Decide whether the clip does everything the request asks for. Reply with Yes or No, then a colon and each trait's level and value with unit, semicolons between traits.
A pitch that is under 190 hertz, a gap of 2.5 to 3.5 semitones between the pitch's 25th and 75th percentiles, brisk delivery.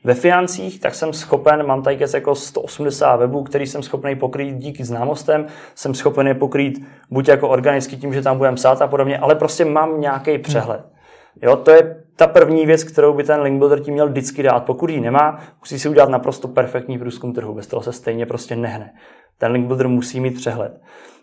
Yes: medium, 140 Hz; average, 2.8 semitones; fast, 205 wpm